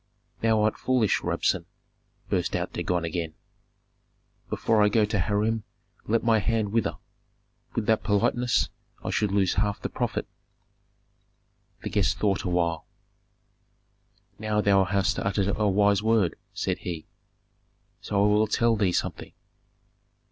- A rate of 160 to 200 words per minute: No, slow, 135 wpm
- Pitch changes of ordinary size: No, narrow, 2.3 semitones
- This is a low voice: Yes, low, 105 Hz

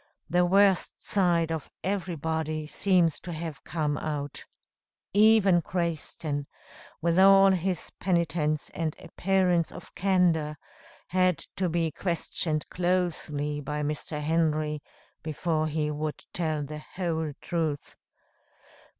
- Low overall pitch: No, medium, 165 Hz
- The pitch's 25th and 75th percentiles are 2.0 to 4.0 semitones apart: Yes, average, 2.9 semitones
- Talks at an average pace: No, slow, 110 wpm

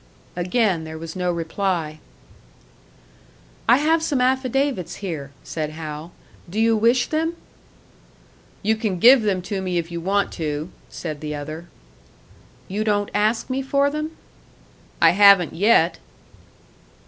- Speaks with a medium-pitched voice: No, high, 195 Hz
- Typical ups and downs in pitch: No, wide, 6.4 semitones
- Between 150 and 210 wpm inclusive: No, slow, 135 wpm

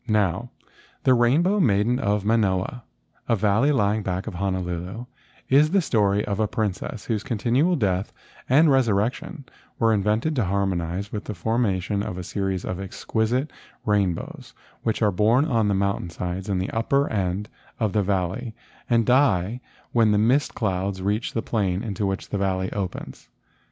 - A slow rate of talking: No, average, 160 wpm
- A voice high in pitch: No, low, 105 Hz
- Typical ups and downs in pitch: Yes, average, 3.6 semitones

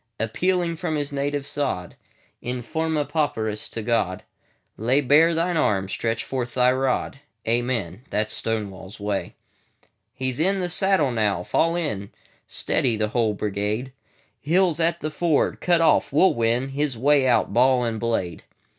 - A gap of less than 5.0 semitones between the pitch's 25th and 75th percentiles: No, wide, 5.6 semitones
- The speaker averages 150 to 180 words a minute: No, slow, 135 wpm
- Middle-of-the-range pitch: No, low, 130 Hz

